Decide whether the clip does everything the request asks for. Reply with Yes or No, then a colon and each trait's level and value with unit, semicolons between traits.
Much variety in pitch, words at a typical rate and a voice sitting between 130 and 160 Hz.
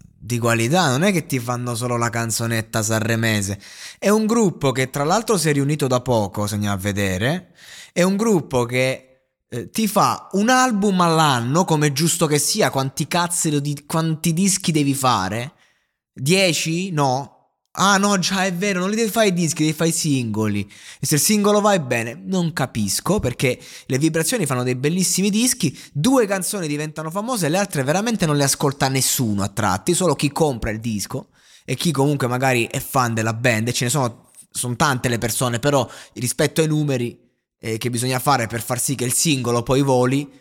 No: wide, 6.1 semitones; fast, 195 wpm; medium, 140 Hz